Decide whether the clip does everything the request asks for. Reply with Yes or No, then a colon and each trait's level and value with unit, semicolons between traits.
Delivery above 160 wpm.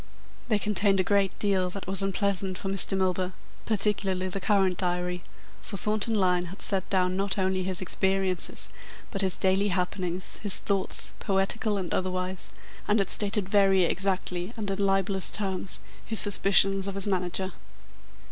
No: average, 155 wpm